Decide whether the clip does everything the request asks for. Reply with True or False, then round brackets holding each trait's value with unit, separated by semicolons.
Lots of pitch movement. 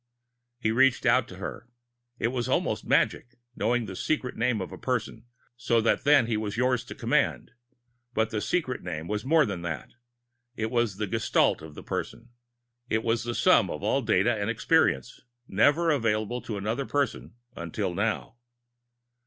False (3.2 semitones)